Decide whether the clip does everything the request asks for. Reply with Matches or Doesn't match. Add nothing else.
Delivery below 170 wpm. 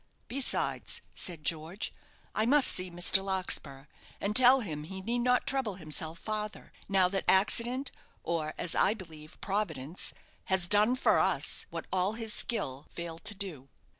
Matches